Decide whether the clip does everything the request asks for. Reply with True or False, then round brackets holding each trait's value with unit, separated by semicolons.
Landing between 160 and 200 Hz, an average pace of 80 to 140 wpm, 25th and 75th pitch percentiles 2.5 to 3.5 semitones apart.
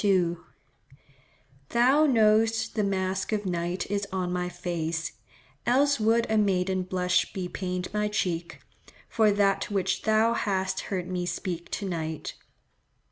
True (190 Hz; 135 wpm; 3.1 semitones)